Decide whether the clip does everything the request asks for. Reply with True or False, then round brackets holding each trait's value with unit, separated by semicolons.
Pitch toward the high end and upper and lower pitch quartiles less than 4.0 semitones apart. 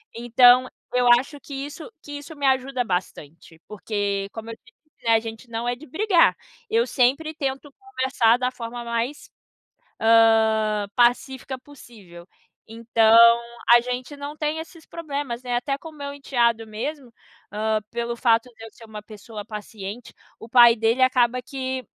True (245 Hz; 3.5 semitones)